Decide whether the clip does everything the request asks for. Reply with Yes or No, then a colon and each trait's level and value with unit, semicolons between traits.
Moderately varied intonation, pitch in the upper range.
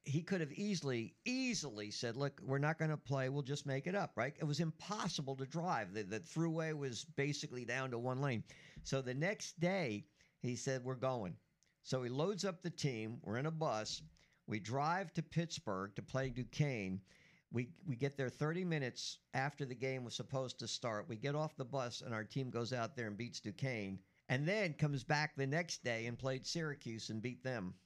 No: average, 4.5 semitones; low, 135 Hz